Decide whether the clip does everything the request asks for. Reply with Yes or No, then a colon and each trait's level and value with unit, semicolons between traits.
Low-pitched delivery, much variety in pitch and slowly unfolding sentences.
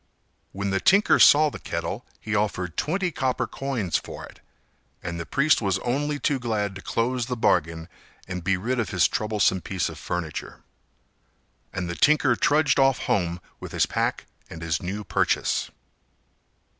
No: low, 105 Hz; wide, 6.8 semitones; average, 165 wpm